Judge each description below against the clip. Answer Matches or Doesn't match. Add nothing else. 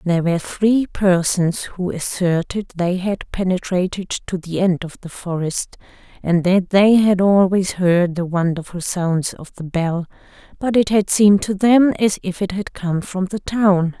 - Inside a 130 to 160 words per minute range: Doesn't match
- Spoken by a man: Doesn't match